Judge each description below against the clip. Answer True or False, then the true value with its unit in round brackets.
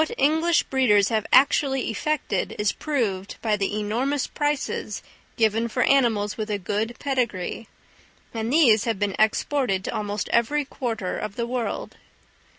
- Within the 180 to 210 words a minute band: False (150 wpm)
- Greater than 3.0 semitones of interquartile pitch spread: True (4.5 semitones)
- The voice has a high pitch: True (230 Hz)